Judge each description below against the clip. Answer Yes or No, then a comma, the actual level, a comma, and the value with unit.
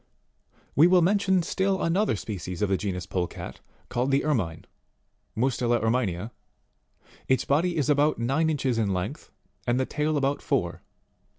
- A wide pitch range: Yes, wide, 6.5 semitones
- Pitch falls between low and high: No, low, 130 Hz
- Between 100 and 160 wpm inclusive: Yes, average, 150 wpm